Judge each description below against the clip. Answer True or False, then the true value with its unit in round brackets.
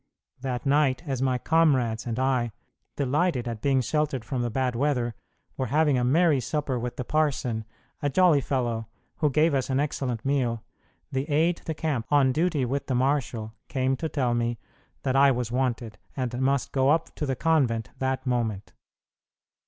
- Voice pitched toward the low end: True (130 Hz)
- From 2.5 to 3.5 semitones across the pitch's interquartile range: True (3.0 semitones)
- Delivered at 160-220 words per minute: True (175 wpm)